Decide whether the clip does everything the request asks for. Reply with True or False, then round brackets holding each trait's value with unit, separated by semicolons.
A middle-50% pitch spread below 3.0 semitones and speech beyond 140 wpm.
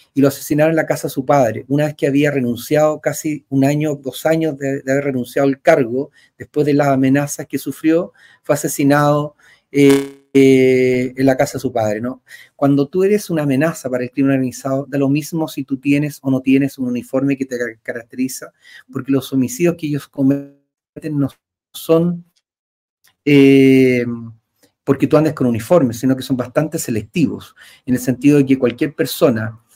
True (2.4 semitones; 185 wpm)